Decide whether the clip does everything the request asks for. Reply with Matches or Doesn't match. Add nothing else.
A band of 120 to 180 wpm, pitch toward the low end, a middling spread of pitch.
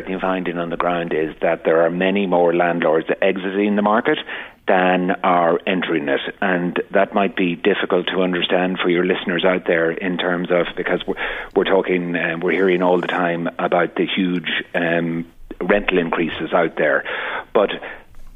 Doesn't match